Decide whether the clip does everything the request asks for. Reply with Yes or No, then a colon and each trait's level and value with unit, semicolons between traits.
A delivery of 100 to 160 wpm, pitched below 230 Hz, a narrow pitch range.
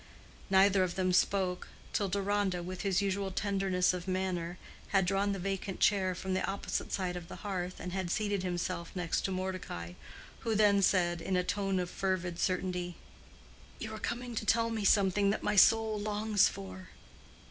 No: average, 180 wpm; high, 190 Hz; narrow, 1.9 semitones